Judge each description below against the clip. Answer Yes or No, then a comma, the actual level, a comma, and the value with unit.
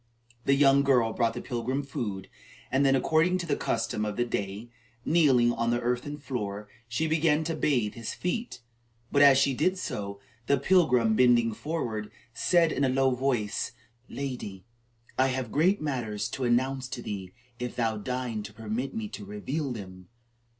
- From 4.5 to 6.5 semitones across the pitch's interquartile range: No, average, 4.1 semitones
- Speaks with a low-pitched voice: Yes, low, 125 Hz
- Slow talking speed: No, average, 170 wpm